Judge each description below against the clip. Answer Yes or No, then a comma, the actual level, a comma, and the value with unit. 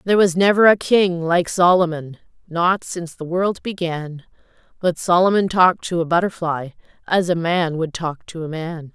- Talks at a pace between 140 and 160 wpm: No, average, 175 wpm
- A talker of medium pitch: Yes, medium, 175 Hz